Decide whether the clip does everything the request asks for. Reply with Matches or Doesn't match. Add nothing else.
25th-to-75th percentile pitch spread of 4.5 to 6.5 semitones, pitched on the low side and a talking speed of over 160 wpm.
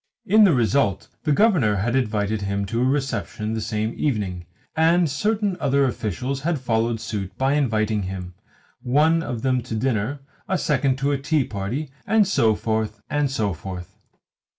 Matches